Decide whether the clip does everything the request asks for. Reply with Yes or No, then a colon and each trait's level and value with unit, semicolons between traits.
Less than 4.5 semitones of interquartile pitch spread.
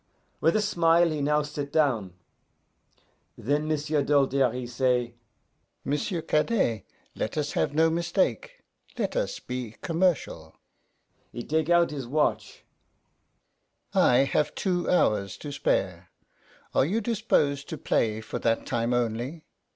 No: average, 5.2 semitones